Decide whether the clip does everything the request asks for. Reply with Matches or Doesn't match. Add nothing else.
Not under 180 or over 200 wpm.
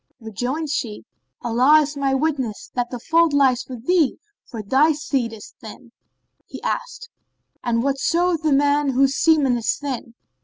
Doesn't match